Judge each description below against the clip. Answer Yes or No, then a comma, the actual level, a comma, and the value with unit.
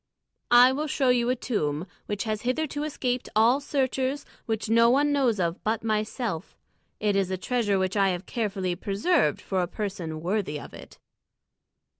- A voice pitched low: No, high, 220 Hz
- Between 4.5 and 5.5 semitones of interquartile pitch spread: Yes, average, 4.8 semitones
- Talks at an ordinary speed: Yes, average, 170 wpm